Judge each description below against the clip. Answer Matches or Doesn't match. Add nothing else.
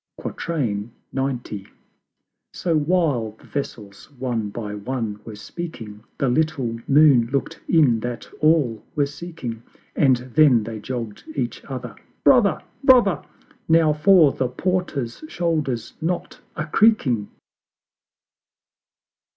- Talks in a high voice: Doesn't match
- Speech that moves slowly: Matches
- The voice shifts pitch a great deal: Matches